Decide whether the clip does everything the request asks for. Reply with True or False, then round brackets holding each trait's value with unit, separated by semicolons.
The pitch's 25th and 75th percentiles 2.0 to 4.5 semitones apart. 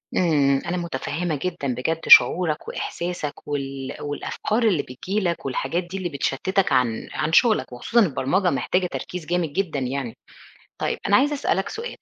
False (5.1 semitones)